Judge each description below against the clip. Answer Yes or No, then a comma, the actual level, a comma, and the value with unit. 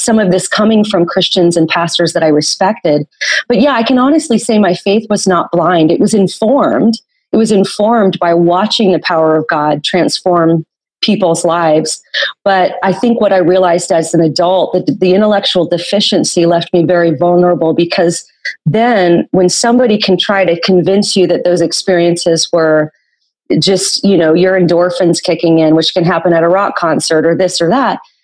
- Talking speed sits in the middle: Yes, average, 180 wpm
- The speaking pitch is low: No, medium, 180 Hz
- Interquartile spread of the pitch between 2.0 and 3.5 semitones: Yes, average, 2.9 semitones